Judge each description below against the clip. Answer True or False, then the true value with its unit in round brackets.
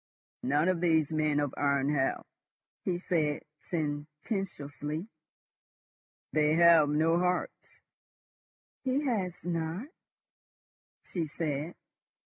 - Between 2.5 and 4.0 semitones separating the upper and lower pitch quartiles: True (3.1 semitones)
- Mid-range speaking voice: True (160 Hz)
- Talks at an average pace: False (90 wpm)